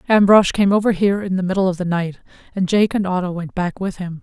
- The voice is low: No, high, 190 Hz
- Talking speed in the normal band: No, fast, 255 wpm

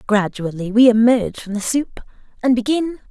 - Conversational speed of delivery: Yes, average, 155 wpm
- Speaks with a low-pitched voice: No, high, 230 Hz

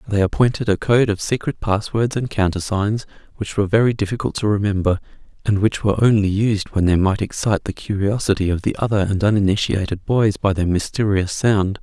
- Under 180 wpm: No, average, 185 wpm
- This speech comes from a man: Yes, male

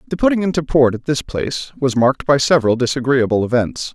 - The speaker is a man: Yes, male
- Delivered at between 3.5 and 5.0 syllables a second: No, 6.2 syllables/s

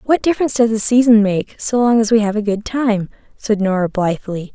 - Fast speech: Yes, fast, 225 wpm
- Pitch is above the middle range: Yes, high, 215 Hz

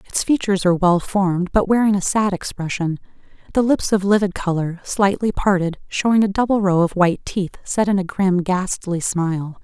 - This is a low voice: No, high, 190 Hz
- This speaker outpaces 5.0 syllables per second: Yes, 5.3 syllables/s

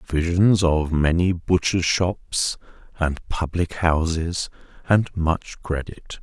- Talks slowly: Yes, slow, 105 wpm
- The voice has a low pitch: Yes, very low, 85 Hz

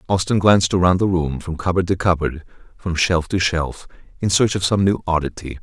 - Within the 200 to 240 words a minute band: Yes, fast, 205 wpm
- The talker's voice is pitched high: No, very low, 90 Hz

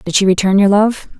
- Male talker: No, female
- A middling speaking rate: No, fast, 250 wpm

